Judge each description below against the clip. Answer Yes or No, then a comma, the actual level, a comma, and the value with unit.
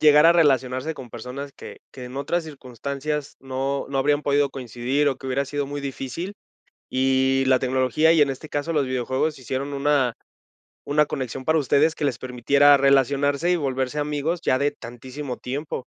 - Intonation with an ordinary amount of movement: No, narrow, 2.1 semitones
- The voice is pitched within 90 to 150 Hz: Yes, medium, 140 Hz